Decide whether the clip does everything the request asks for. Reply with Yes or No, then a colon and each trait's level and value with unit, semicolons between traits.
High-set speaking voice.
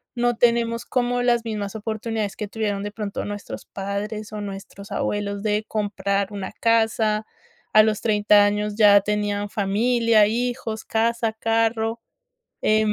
Yes: high, 215 Hz